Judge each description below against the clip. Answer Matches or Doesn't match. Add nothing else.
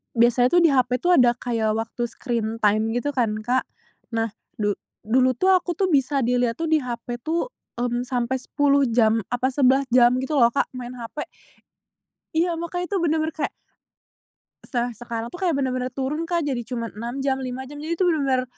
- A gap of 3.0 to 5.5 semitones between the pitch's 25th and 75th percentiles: Matches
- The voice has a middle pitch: Doesn't match